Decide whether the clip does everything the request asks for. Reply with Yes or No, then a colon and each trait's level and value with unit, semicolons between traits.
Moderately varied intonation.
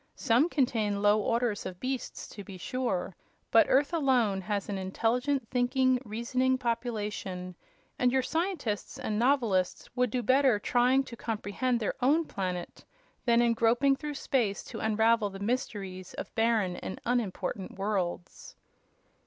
Yes: average, 4.0 semitones